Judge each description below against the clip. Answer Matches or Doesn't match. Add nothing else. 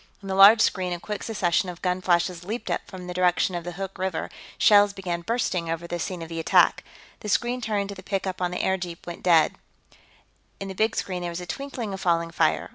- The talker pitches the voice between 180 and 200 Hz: Matches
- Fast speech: Matches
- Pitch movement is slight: Matches